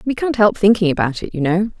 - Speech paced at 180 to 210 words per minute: No, fast, 265 wpm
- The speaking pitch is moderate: No, high, 195 Hz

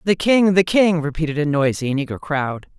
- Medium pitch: Yes, medium, 160 Hz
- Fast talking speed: Yes, fast, 215 wpm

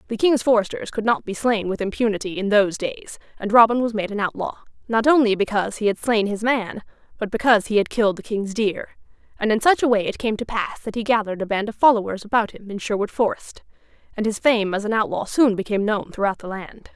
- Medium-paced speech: No, fast, 235 wpm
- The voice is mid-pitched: No, high, 215 Hz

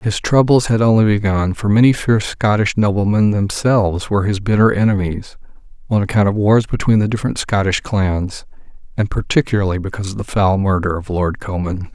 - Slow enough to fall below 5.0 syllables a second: No, 5.6 syllables/s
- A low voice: Yes, low, 100 Hz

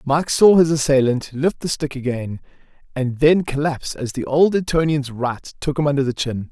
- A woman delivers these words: No, male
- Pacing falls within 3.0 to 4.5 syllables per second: No, 5.0 syllables/s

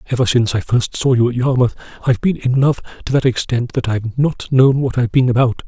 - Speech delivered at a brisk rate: Yes, fast, 245 wpm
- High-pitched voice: No, low, 125 Hz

